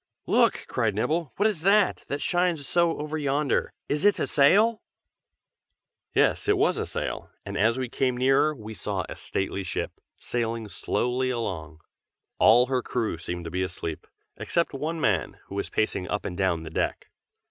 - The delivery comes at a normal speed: Yes, average, 175 wpm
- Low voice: Yes, low, 125 Hz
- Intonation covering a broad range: Yes, wide, 7.6 semitones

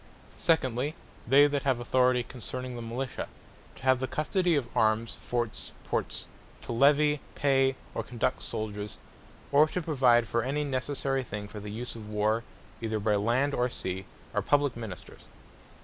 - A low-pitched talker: Yes, low, 125 Hz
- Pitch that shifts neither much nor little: Yes, average, 3.7 semitones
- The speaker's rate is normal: Yes, average, 160 wpm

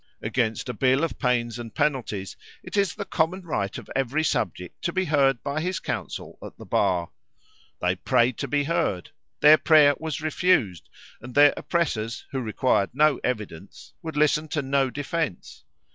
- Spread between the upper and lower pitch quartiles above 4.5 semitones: Yes, average, 4.9 semitones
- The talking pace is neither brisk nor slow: Yes, average, 170 wpm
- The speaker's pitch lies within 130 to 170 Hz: Yes, medium, 140 Hz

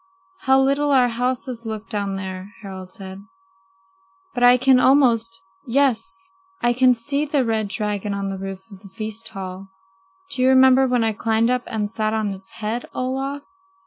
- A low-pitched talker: No, high, 230 Hz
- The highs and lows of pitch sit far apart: No, average, 4.2 semitones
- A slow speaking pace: No, average, 175 wpm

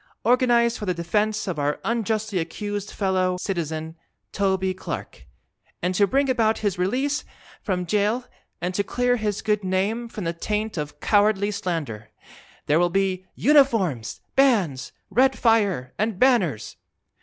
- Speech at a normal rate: Yes, average, 145 wpm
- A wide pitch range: No, average, 4.0 semitones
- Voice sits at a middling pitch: No, high, 200 Hz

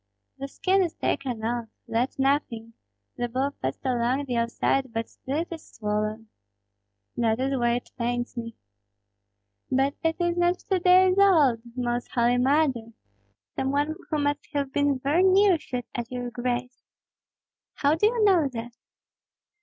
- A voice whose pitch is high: Yes, very high, 265 Hz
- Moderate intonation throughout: Yes, average, 4.6 semitones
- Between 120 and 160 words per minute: Yes, average, 155 wpm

